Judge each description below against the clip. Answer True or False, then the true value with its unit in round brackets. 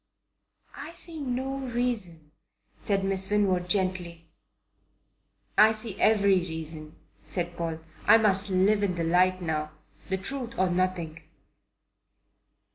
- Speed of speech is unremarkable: False (120 wpm)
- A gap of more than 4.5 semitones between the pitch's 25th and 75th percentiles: False (3.9 semitones)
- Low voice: False (185 Hz)